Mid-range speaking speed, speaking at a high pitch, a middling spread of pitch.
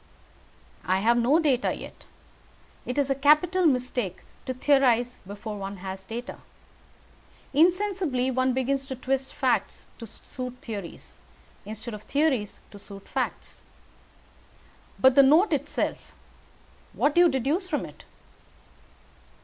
No: slow, 125 wpm; very high, 255 Hz; average, 4.4 semitones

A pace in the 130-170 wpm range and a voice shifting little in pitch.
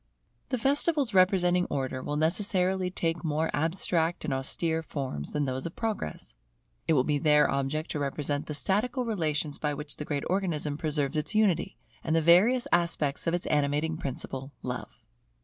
No: average, 165 wpm; average, 3.9 semitones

